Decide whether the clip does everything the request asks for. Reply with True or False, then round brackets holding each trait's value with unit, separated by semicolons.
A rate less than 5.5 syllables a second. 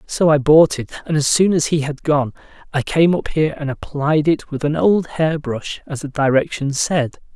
True (4.8 syllables/s)